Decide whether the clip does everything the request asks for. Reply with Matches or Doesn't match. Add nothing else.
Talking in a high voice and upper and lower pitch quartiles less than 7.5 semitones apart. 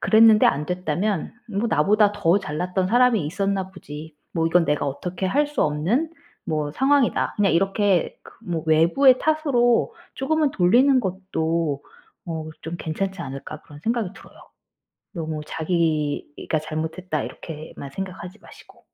Doesn't match